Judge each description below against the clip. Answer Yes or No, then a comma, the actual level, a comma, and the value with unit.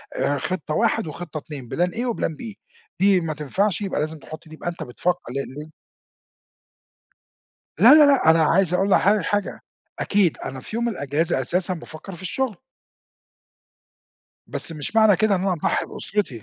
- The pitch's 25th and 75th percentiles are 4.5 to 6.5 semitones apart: Yes, average, 4.8 semitones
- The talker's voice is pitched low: No, medium, 175 Hz